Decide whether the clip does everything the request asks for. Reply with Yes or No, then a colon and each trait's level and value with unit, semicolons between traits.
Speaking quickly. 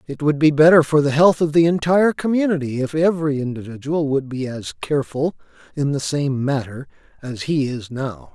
No: average, 185 wpm